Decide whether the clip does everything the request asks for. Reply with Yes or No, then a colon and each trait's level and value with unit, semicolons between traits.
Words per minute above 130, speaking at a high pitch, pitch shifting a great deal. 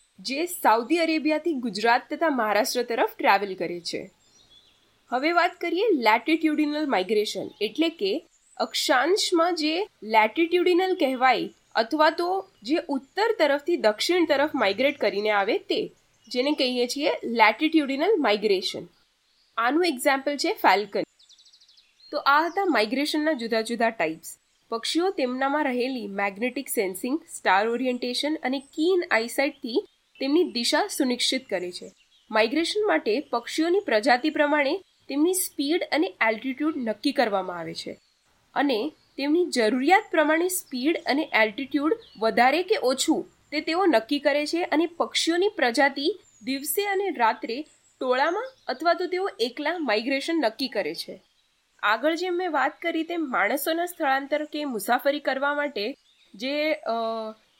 No: average, 125 wpm; very high, 290 Hz; wide, 5.8 semitones